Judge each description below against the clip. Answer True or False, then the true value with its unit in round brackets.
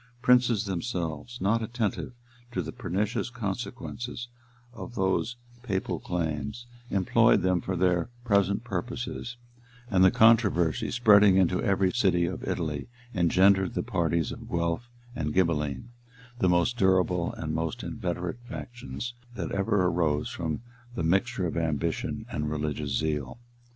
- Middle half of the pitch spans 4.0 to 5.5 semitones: True (5.2 semitones)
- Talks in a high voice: False (95 Hz)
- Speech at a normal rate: False (130 wpm)